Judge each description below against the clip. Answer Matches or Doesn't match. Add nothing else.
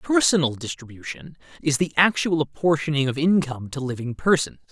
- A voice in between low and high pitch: Matches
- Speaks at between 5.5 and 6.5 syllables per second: Matches